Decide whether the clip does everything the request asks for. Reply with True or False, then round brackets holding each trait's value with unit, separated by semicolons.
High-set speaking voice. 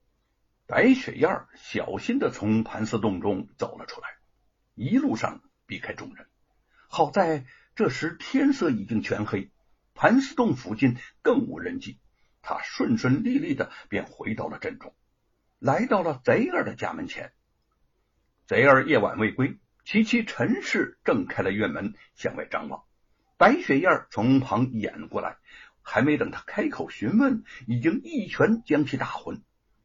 False (150 Hz)